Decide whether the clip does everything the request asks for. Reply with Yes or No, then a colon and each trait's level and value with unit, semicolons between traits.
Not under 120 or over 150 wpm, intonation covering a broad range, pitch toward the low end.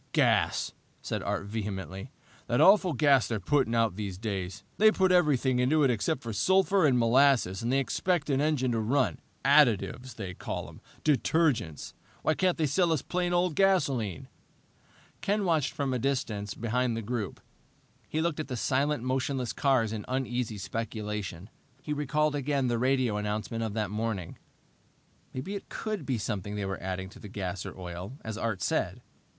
No: average, 170 wpm; wide, 5.8 semitones; low, 125 Hz